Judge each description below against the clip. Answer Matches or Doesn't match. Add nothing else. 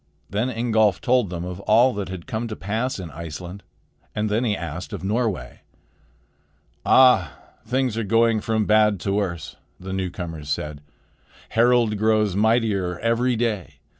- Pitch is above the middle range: Doesn't match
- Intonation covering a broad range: Doesn't match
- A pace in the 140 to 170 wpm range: Matches